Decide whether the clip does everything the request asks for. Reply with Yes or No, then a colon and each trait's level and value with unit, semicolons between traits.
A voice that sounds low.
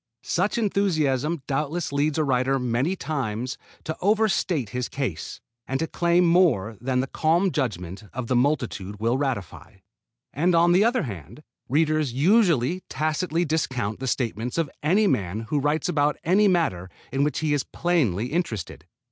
No: medium, 145 Hz